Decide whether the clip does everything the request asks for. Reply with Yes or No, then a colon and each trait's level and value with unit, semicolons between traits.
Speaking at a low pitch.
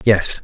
Yes: low, 105 Hz